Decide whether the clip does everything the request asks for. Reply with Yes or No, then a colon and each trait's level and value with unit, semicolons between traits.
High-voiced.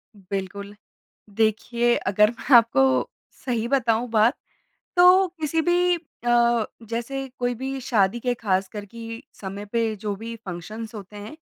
Yes: high, 230 Hz